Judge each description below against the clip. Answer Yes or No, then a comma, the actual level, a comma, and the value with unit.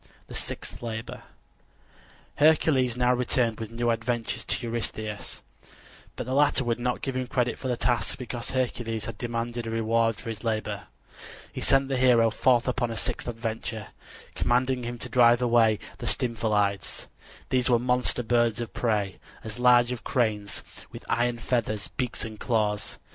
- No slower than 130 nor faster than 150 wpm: No, average, 165 wpm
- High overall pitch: No, low, 120 Hz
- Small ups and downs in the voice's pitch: Yes, narrow, 1.7 semitones